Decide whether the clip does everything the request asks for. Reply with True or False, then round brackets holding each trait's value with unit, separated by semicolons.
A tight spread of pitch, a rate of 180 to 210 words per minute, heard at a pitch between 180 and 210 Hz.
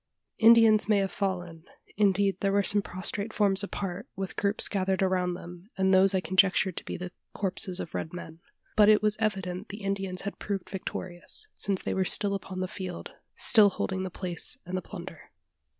True (1.7 semitones; 190 wpm; 190 Hz)